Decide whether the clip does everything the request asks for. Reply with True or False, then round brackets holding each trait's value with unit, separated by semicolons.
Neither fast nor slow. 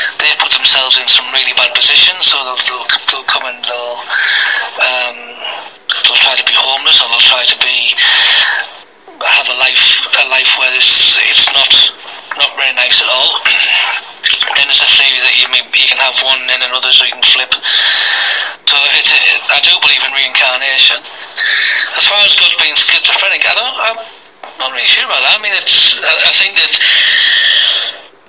True (180 wpm)